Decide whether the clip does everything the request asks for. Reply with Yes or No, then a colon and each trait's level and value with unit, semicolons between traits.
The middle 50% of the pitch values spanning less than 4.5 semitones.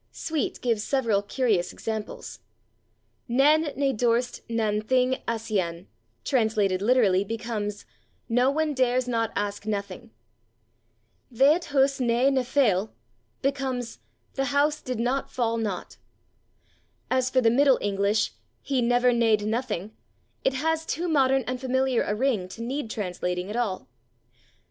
Yes: average, 4.0 semitones